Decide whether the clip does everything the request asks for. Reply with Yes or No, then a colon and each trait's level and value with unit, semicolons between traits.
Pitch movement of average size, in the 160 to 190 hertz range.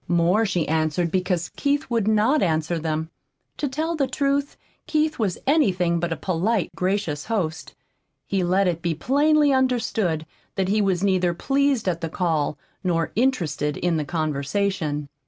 No: wide, 6.3 semitones; medium, 185 Hz